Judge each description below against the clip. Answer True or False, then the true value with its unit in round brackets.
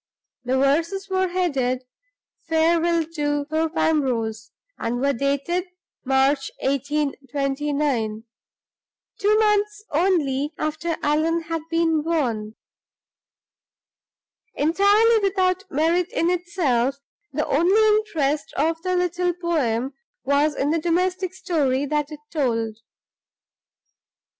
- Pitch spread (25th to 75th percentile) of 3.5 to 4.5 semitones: True (4.2 semitones)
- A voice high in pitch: True (310 Hz)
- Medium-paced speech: False (100 wpm)